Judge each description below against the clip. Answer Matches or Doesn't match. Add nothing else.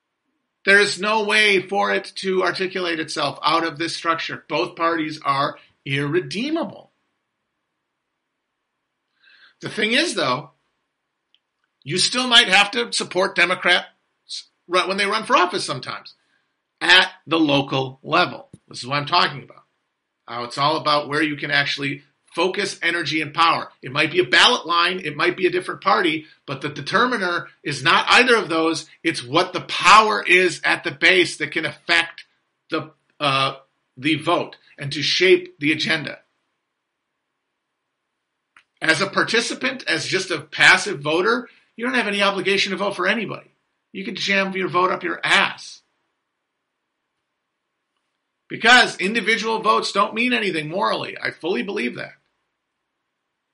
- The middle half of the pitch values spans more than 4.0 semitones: Matches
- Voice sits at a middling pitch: Matches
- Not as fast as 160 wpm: Matches